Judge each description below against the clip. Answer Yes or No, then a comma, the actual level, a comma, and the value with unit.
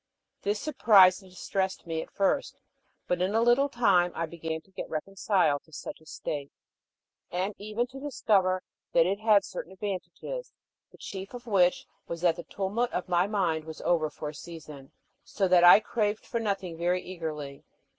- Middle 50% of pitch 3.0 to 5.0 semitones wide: Yes, average, 3.8 semitones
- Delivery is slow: No, average, 180 wpm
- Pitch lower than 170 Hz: No, medium, 185 Hz